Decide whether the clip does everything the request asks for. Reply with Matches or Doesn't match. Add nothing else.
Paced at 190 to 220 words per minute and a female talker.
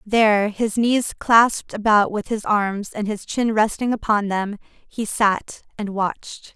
Doesn't match